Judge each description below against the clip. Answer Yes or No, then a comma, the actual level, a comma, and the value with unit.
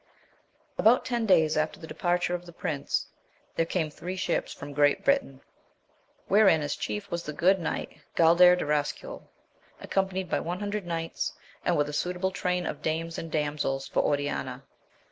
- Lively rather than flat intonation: No, average, 3.6 semitones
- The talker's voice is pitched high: No, medium, 170 Hz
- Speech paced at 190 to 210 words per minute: No, average, 160 wpm